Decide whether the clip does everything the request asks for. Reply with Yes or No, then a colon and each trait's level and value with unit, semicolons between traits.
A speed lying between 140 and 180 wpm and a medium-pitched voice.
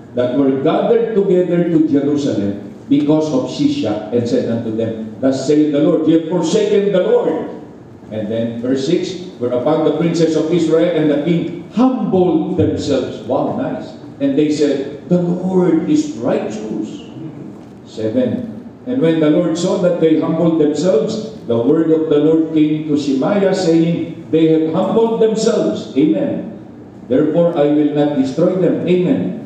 Yes: fast, 155 wpm; medium, 160 Hz